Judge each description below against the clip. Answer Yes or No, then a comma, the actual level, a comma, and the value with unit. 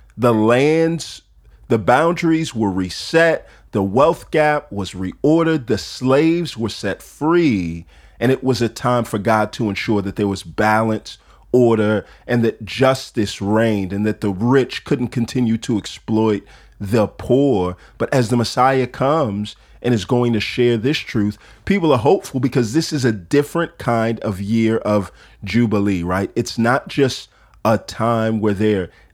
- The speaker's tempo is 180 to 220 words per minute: No, average, 160 wpm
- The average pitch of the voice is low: Yes, low, 115 Hz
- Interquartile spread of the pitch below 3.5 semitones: No, average, 3.9 semitones